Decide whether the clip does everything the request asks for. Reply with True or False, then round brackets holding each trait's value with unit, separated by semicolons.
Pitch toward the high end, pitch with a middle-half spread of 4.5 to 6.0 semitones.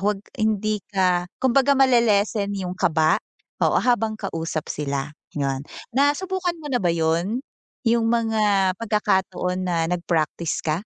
True (200 Hz; 5.3 semitones)